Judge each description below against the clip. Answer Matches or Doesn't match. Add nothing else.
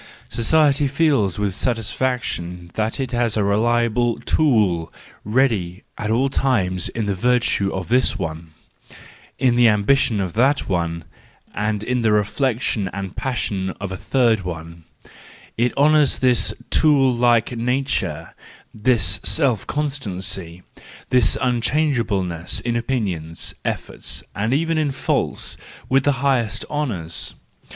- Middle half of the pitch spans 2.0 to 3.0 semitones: Doesn't match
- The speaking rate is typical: Doesn't match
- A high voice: Doesn't match